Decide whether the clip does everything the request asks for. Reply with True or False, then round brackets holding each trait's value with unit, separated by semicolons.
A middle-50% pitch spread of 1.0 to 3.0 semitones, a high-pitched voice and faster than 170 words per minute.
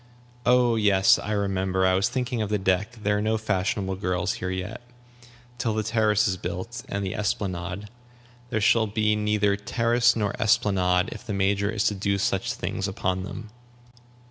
False (2.6 semitones; 105 Hz; 180 wpm)